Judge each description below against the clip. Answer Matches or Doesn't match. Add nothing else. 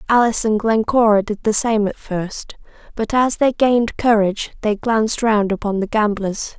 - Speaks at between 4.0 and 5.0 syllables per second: Matches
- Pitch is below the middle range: Doesn't match